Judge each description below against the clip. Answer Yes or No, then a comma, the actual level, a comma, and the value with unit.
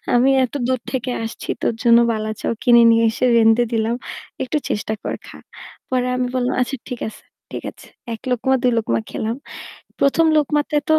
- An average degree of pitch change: No, narrow, 2.3 semitones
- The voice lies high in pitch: Yes, high, 240 Hz